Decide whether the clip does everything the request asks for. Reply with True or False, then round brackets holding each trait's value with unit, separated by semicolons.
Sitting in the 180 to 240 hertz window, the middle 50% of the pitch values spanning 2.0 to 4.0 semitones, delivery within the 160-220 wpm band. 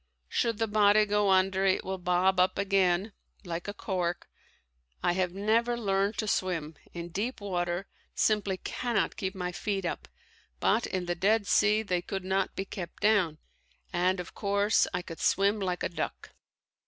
True (190 Hz; 2.5 semitones; 170 wpm)